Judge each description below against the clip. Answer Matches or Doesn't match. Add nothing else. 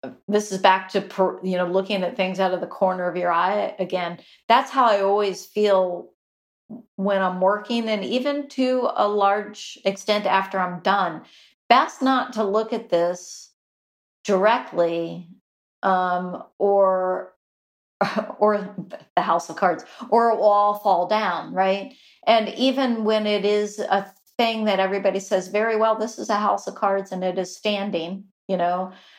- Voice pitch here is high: Matches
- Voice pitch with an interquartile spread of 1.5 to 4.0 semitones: Matches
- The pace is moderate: Matches